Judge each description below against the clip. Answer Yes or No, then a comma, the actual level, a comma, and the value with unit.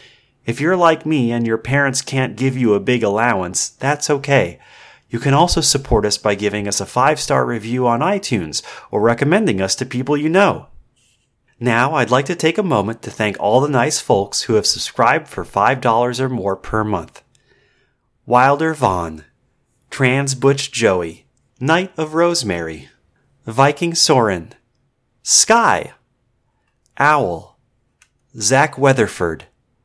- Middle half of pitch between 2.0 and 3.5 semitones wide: No, average, 4.0 semitones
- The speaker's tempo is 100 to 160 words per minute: Yes, average, 145 wpm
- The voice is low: Yes, low, 125 Hz